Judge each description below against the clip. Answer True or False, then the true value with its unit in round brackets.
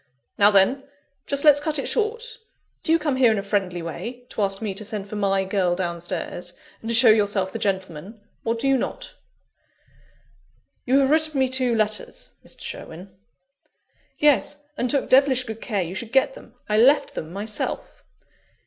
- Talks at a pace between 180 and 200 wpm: True (185 wpm)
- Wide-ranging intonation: True (5.7 semitones)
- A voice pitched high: True (220 Hz)